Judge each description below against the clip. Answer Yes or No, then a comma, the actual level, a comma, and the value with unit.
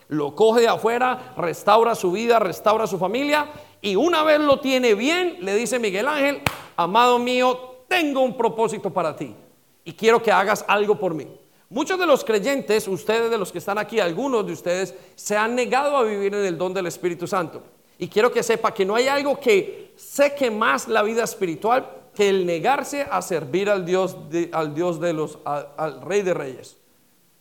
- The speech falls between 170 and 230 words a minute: Yes, average, 190 wpm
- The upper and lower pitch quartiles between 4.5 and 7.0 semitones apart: Yes, wide, 5.5 semitones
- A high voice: Yes, high, 215 Hz